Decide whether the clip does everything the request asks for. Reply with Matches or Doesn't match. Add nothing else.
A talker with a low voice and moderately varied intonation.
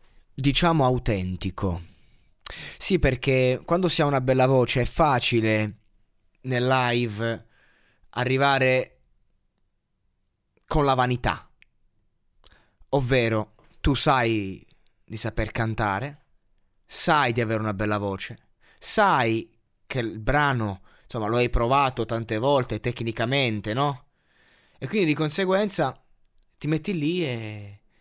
Matches